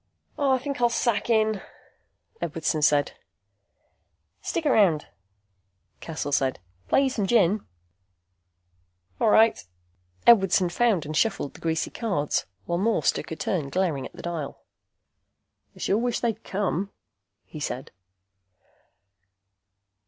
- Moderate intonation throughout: No, wide, 6.4 semitones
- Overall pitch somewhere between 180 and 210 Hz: Yes, high, 190 Hz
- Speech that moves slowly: Yes, slow, 120 wpm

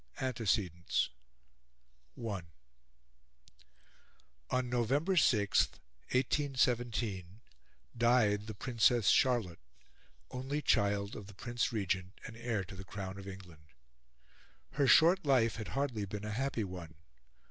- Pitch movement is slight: No, average, 4.5 semitones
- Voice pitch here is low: Yes, low, 110 Hz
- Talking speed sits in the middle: No, slow, 110 wpm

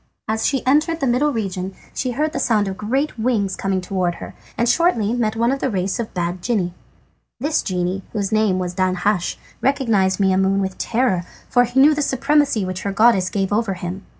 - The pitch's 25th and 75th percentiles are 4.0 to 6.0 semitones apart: Yes, average, 5.1 semitones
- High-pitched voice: Yes, high, 215 Hz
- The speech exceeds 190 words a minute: Yes, fast, 205 wpm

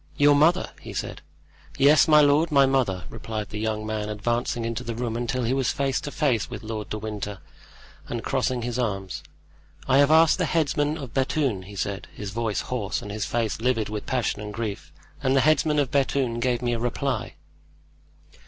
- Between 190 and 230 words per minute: Yes, average, 195 wpm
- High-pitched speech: No, low, 120 Hz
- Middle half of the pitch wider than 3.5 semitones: Yes, average, 4.4 semitones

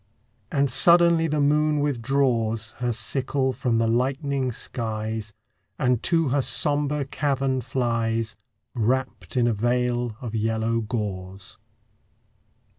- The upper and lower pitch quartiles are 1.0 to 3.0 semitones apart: No, average, 3.7 semitones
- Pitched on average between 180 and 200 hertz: No, low, 125 Hz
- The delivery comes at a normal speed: No, slow, 115 wpm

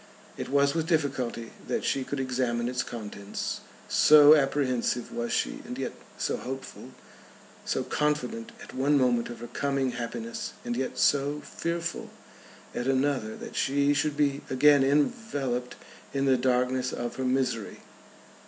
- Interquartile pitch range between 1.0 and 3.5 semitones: Yes, average, 2.7 semitones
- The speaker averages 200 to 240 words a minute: No, average, 145 wpm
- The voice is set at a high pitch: No, low, 135 Hz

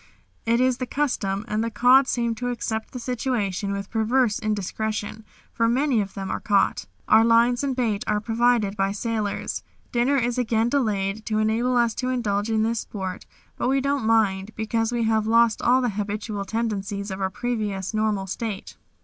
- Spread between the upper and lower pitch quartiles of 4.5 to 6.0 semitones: No, average, 2.8 semitones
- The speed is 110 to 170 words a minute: No, average, 185 wpm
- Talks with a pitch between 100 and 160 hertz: No, high, 220 Hz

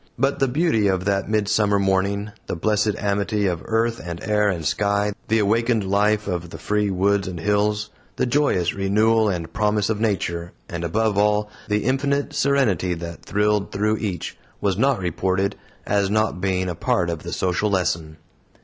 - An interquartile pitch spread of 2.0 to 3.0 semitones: Yes, narrow, 2.4 semitones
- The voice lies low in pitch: Yes, low, 100 Hz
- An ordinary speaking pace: Yes, average, 175 wpm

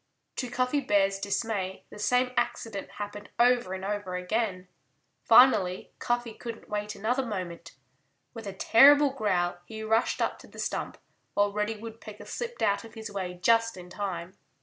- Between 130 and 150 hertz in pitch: No, high, 210 Hz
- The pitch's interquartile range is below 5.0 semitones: Yes, average, 3.2 semitones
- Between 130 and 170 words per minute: Yes, average, 160 wpm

